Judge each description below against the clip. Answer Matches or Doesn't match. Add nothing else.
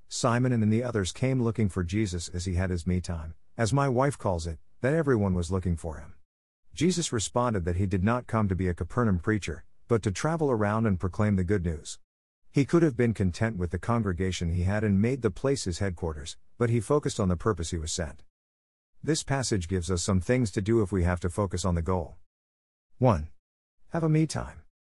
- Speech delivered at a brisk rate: Matches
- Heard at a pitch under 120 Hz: Matches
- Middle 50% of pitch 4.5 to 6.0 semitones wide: Matches